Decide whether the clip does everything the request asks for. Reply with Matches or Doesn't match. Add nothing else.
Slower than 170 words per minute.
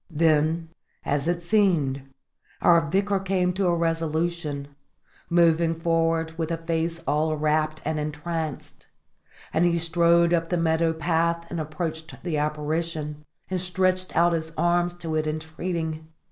Matches